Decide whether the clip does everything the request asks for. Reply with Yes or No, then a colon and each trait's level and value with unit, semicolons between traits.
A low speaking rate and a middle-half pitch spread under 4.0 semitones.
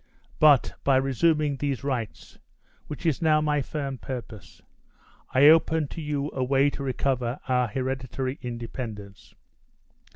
Yes: slow, 130 wpm; average, 2.8 semitones